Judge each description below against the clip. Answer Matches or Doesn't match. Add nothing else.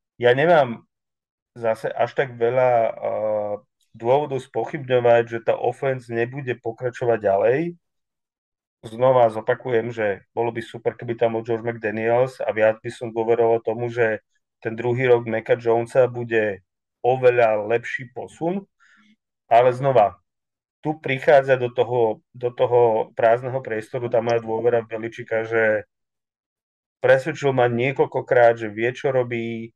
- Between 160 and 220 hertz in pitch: Doesn't match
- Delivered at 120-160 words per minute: Matches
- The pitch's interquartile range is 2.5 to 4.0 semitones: Doesn't match